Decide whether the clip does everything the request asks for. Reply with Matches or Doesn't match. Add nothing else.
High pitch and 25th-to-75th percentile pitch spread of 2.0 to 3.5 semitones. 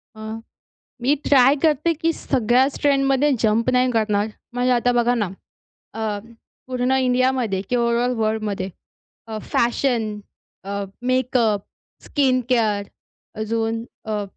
Matches